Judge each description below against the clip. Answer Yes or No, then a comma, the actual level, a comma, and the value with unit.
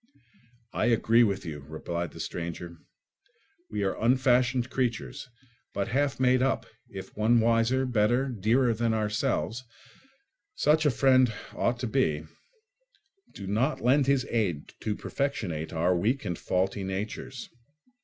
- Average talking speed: No, slow, 125 wpm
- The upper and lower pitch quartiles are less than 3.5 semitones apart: No, average, 5.2 semitones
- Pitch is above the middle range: No, low, 115 Hz